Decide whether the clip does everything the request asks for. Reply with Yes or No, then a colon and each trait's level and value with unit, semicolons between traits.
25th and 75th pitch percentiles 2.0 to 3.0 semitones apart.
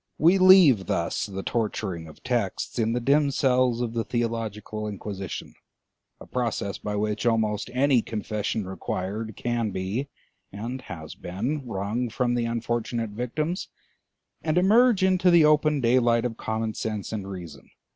No: average, 3.6 semitones